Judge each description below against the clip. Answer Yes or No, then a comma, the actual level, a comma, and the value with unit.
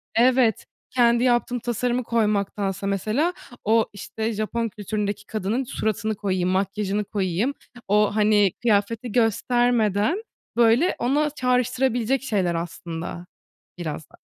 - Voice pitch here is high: Yes, high, 220 Hz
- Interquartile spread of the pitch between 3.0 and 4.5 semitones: Yes, average, 3.3 semitones